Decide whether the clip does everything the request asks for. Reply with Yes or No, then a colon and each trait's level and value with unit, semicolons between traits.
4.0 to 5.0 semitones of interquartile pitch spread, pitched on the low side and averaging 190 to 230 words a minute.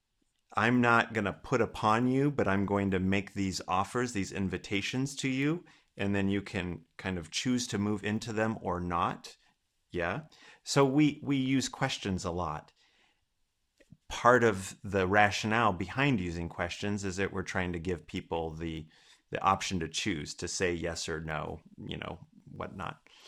No: average, 4.6 semitones; low, 100 Hz; average, 170 wpm